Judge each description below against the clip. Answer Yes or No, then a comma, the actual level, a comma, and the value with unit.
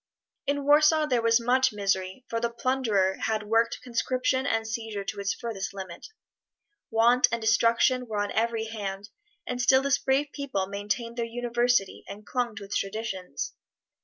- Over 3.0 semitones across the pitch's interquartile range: Yes, average, 3.4 semitones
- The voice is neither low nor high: No, high, 230 Hz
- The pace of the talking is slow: No, average, 160 wpm